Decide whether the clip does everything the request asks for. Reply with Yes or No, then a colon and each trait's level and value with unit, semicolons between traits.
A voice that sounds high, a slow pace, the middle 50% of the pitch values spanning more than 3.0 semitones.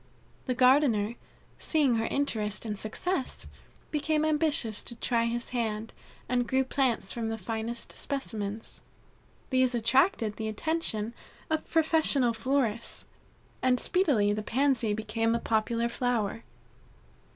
Yes: high, 235 Hz; slow, 120 wpm; average, 3.7 semitones